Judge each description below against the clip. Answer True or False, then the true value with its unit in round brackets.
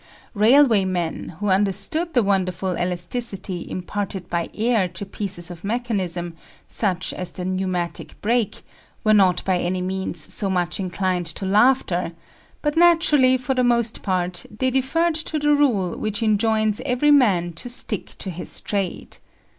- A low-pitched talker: False (200 Hz)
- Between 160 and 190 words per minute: False (150 wpm)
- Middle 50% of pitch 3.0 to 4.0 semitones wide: False (5.1 semitones)